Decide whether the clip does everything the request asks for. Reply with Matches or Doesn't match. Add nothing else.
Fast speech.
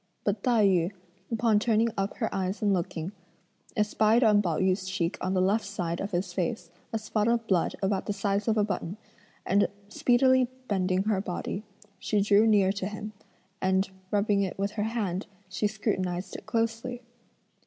Doesn't match